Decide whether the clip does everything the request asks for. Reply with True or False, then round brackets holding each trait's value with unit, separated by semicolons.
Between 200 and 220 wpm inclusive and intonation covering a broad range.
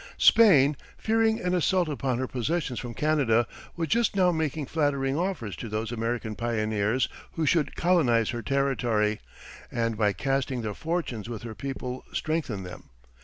False (155 wpm; 5.8 semitones)